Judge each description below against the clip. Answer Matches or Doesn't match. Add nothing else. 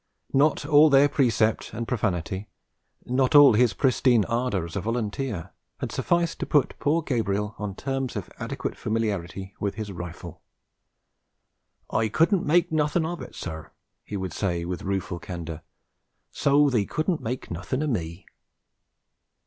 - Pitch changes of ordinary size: Doesn't match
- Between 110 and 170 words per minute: Matches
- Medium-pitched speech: Doesn't match